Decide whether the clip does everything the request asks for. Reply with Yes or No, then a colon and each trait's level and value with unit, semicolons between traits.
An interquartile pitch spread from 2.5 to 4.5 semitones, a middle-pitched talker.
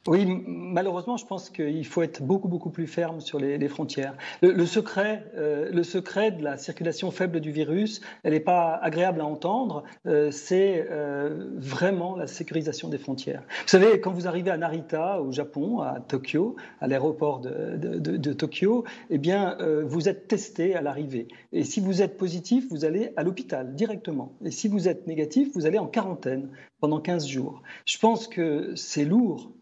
Yes: average, 4.1 semitones; medium, 170 Hz